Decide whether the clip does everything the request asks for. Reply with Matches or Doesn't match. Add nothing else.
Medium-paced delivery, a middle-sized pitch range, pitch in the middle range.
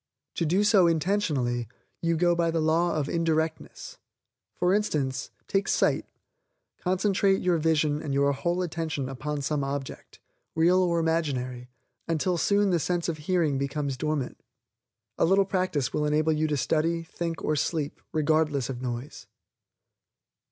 Matches